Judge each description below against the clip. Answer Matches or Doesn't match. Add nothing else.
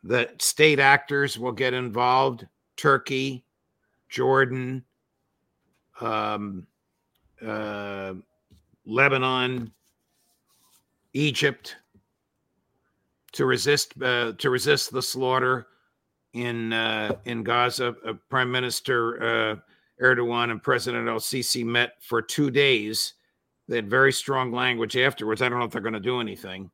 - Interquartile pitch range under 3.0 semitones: Matches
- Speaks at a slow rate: Matches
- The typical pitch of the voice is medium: Doesn't match